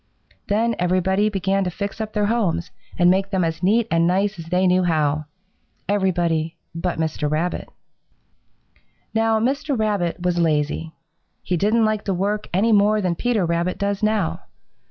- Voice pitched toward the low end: No, high, 190 Hz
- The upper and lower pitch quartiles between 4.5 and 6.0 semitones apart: No, average, 3.6 semitones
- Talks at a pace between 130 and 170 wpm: Yes, average, 160 wpm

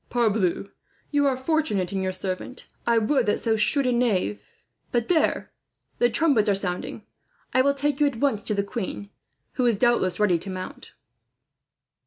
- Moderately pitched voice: No, high, 225 Hz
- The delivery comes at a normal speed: Yes, average, 170 wpm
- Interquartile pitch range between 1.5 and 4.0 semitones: No, average, 5.1 semitones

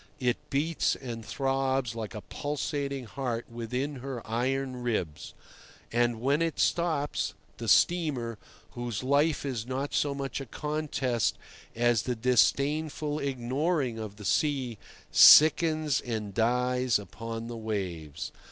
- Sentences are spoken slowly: Yes, slow, 125 wpm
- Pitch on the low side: Yes, low, 125 Hz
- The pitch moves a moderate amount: Yes, average, 3.6 semitones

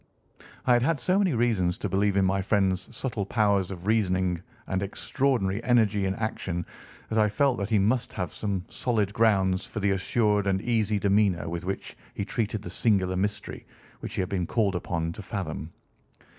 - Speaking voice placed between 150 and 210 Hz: No, low, 100 Hz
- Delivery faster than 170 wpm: Yes, average, 185 wpm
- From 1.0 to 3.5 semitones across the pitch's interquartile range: Yes, average, 2.8 semitones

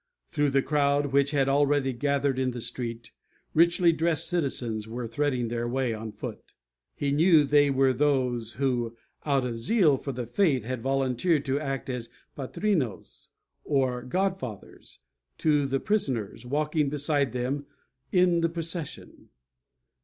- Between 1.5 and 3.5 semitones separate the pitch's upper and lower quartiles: Yes, average, 3.2 semitones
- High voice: No, low, 135 Hz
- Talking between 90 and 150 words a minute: Yes, average, 145 wpm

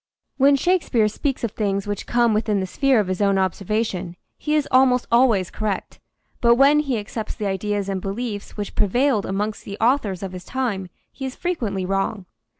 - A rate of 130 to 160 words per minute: No, average, 185 wpm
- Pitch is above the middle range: Yes, high, 215 Hz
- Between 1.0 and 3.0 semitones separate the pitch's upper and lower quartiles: No, average, 4.5 semitones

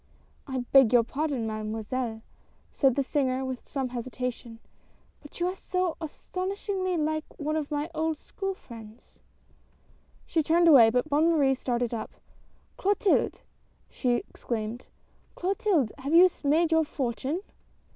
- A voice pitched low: No, very high, 280 Hz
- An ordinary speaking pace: Yes, average, 155 wpm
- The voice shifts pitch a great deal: No, average, 5.0 semitones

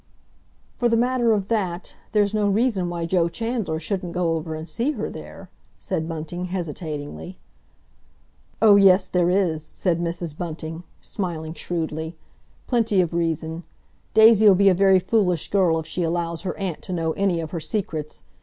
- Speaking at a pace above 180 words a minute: No, average, 165 wpm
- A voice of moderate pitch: Yes, medium, 175 Hz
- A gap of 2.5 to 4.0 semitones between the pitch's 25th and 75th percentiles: Yes, average, 3.6 semitones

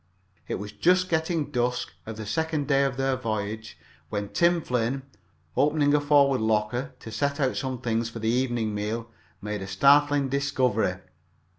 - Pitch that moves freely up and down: No, average, 4.4 semitones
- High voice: No, low, 130 Hz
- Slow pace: No, average, 165 wpm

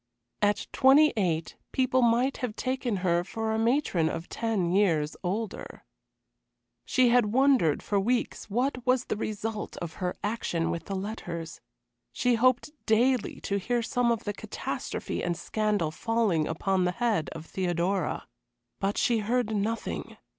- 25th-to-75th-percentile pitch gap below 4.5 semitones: No, average, 5.1 semitones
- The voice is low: No, high, 215 Hz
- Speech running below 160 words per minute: Yes, average, 145 wpm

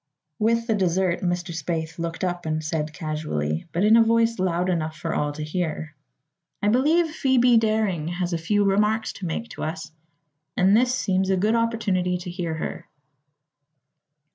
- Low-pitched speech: No, medium, 180 Hz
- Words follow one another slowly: No, average, 170 wpm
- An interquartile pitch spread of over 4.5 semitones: Yes, average, 5.3 semitones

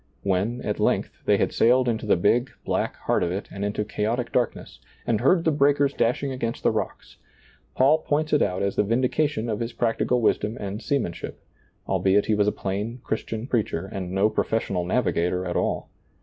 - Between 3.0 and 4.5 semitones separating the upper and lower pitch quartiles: Yes, average, 4.1 semitones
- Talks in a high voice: No, low, 115 Hz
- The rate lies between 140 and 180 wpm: No, average, 190 wpm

